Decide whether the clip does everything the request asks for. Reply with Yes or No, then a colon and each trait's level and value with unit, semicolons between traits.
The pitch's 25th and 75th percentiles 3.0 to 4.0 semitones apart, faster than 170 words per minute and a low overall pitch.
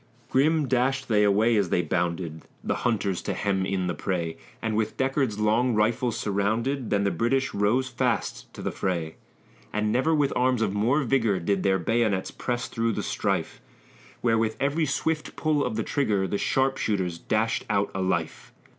No: average, 4.6 semitones; average, 180 wpm; low, 110 Hz